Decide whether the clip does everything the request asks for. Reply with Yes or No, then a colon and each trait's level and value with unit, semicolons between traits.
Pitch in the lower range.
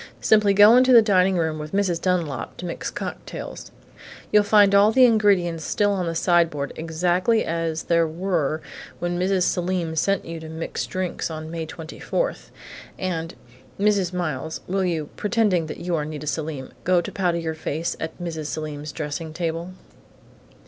No: medium, 170 Hz